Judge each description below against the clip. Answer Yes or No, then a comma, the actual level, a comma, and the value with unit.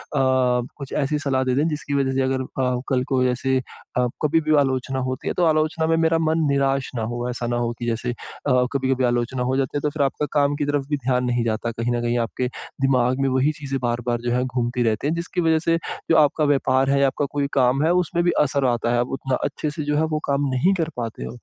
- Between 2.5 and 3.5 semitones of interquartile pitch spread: Yes, average, 2.9 semitones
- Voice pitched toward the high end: No, low, 135 Hz